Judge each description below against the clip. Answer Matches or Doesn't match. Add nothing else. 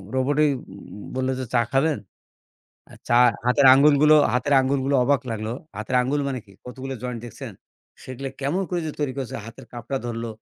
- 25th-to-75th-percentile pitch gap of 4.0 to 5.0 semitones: Doesn't match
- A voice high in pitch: Doesn't match